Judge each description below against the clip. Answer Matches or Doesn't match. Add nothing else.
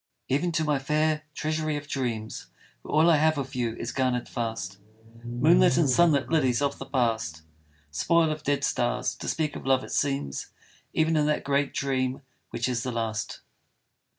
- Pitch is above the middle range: Doesn't match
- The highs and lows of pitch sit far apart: Doesn't match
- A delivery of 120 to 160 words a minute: Doesn't match